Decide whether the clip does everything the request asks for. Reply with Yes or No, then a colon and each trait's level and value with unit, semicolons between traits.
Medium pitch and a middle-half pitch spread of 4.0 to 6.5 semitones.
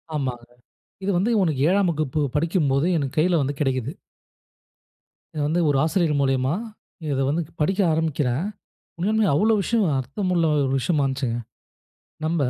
Yes: medium, 155 Hz; average, 4.5 semitones